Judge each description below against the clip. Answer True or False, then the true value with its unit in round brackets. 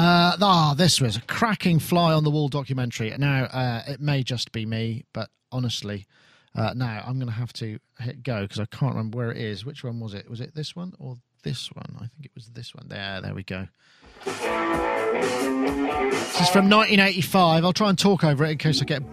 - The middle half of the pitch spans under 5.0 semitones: False (5.3 semitones)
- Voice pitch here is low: True (130 Hz)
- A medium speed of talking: False (225 wpm)